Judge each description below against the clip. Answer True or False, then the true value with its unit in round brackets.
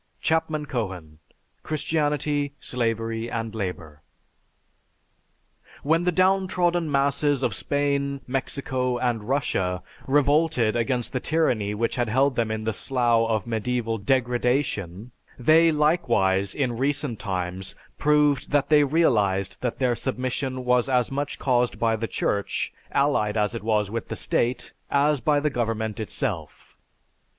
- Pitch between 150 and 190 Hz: False (125 Hz)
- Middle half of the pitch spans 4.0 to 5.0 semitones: True (4.3 semitones)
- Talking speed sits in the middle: False (130 wpm)